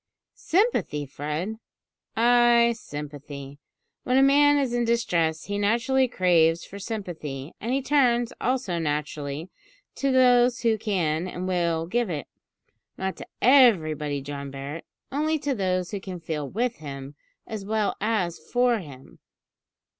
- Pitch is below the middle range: No, high, 190 Hz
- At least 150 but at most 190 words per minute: No, average, 140 wpm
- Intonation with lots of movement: Yes, wide, 7.7 semitones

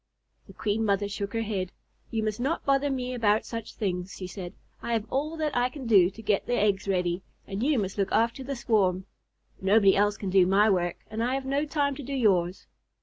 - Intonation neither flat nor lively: Yes, average, 4.4 semitones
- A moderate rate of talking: No, fast, 225 wpm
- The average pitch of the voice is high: Yes, high, 215 Hz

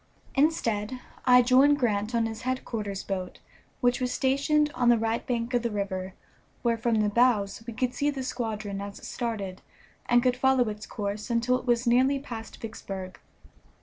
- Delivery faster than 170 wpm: Yes, average, 180 wpm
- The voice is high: Yes, high, 235 Hz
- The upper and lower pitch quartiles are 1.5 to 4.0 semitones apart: Yes, average, 3.2 semitones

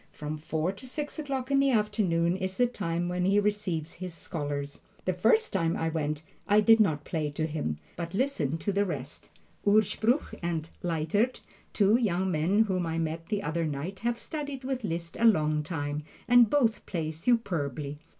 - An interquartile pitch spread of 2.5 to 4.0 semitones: No, wide, 5.5 semitones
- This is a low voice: No, medium, 180 Hz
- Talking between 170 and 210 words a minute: Yes, average, 180 wpm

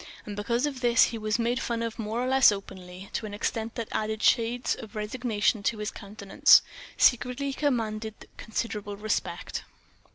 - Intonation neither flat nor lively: No, narrow, 2.3 semitones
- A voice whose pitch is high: Yes, high, 220 Hz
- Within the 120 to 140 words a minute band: No, average, 175 wpm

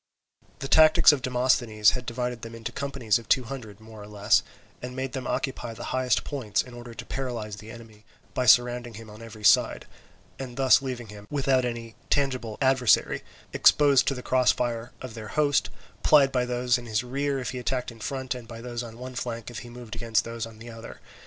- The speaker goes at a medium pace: No, fast, 210 wpm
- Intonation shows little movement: Yes, narrow, 2.2 semitones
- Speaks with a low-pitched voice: Yes, low, 120 Hz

